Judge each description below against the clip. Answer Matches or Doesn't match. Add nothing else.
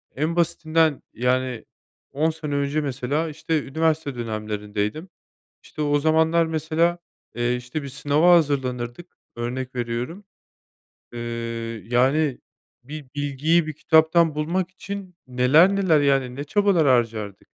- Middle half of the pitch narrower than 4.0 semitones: Doesn't match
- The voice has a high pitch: Doesn't match